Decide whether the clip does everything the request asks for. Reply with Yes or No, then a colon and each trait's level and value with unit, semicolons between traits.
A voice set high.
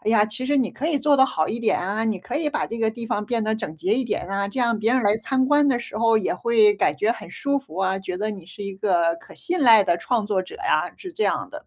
Yes: high, 220 Hz